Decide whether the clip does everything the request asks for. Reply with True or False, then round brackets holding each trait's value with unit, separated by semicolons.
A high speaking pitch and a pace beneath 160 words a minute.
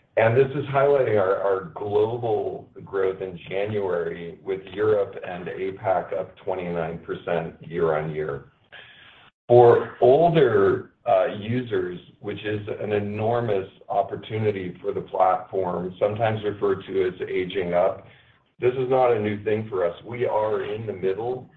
False (140 Hz; 140 wpm)